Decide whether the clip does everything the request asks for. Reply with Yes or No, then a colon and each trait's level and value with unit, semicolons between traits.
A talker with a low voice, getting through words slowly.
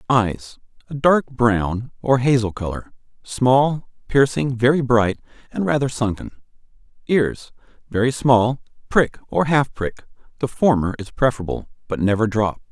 Yes: low, 125 Hz; slow, 125 wpm